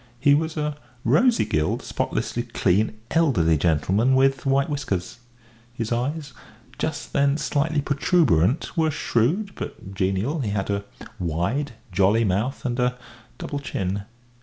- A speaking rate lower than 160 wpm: Yes, slow, 135 wpm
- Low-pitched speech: Yes, low, 125 Hz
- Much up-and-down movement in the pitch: Yes, wide, 6.8 semitones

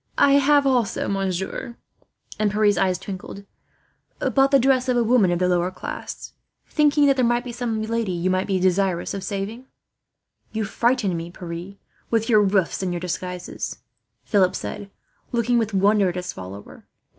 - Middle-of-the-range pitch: No, high, 200 Hz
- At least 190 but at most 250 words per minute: No, average, 170 wpm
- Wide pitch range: No, average, 4.5 semitones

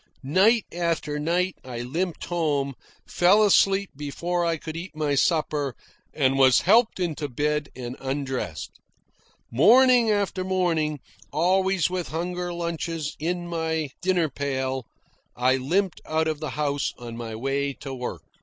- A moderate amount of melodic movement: Yes, average, 4.5 semitones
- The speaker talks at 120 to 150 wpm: Yes, average, 140 wpm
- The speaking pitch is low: No, medium, 160 Hz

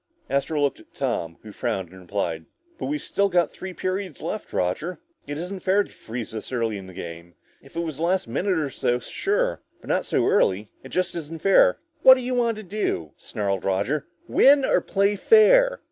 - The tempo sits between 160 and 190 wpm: No, fast, 205 wpm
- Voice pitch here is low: No, medium, 160 Hz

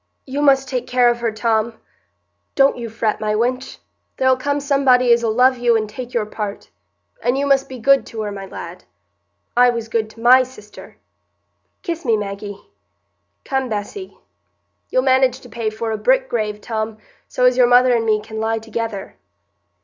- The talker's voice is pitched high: Yes, high, 240 Hz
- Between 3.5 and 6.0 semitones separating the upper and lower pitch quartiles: No, average, 3.0 semitones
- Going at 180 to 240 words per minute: No, average, 165 wpm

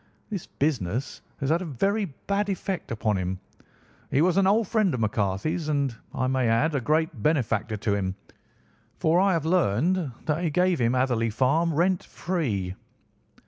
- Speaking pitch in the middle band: Yes, medium, 150 Hz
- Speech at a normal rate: Yes, average, 170 wpm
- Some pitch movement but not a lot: No, wide, 7.5 semitones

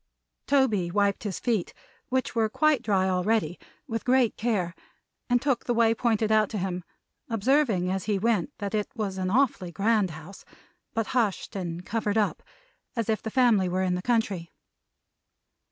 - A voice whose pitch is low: No, high, 215 Hz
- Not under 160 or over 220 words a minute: Yes, average, 170 wpm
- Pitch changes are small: No, average, 3.7 semitones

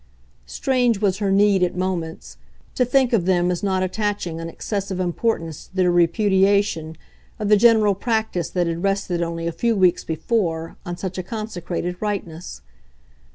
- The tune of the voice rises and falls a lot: No, average, 3.3 semitones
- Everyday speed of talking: Yes, average, 160 wpm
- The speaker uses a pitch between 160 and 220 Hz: Yes, high, 190 Hz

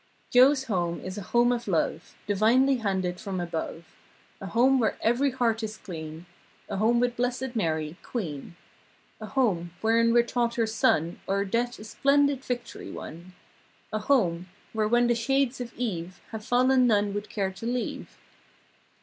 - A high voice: Yes, high, 225 Hz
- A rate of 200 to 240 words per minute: No, average, 165 wpm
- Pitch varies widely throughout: No, average, 4.6 semitones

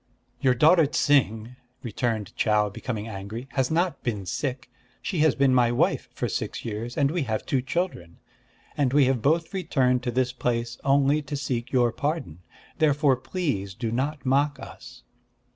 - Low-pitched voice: Yes, low, 130 Hz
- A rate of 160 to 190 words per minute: Yes, average, 165 wpm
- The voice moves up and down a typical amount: Yes, average, 3.7 semitones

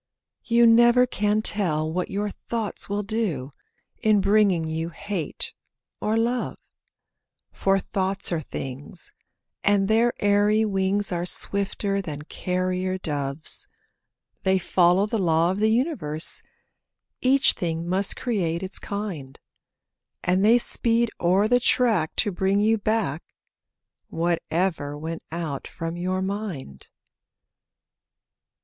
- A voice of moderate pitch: No, high, 195 Hz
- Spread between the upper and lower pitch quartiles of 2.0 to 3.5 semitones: No, average, 4.2 semitones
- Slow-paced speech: Yes, slow, 120 wpm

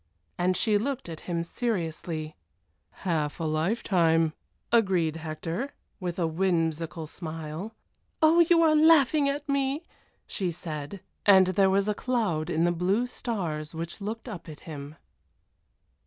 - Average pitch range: No, wide, 6.1 semitones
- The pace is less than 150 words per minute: Yes, average, 140 wpm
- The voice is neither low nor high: Yes, medium, 180 Hz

